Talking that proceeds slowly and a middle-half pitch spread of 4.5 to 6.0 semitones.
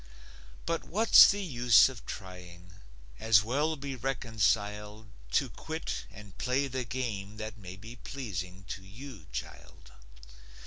Yes: slow, 130 wpm; average, 5.1 semitones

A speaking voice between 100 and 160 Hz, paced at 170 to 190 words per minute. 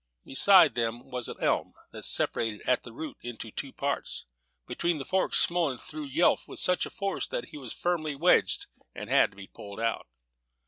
Yes: medium, 140 Hz; average, 185 wpm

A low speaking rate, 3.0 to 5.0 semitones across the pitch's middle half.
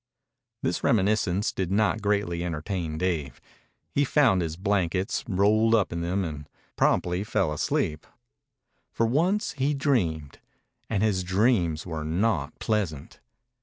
Yes: slow, 130 wpm; average, 4.5 semitones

